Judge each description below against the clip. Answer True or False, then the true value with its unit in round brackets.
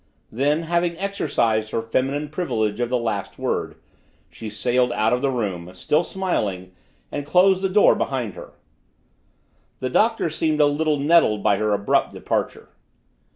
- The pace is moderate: True (155 wpm)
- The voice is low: True (130 Hz)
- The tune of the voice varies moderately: False (6.9 semitones)